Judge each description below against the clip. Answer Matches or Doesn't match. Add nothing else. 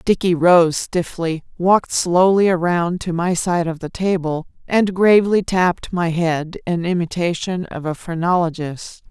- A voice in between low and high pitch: Matches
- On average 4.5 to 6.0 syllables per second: Doesn't match